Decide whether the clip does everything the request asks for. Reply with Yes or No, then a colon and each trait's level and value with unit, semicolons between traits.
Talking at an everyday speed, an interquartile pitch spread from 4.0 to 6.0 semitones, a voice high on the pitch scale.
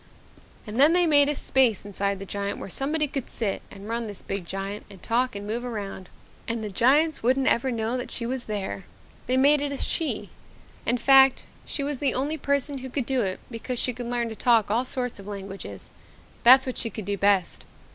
No: fast, 215 wpm; average, 4.7 semitones; high, 240 Hz